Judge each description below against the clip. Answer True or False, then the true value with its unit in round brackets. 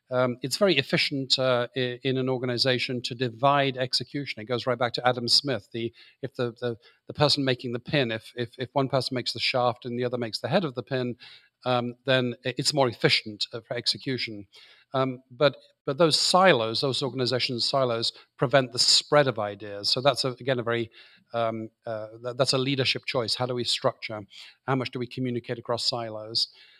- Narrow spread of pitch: True (2.3 semitones)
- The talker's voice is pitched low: True (125 Hz)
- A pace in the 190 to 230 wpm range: True (200 wpm)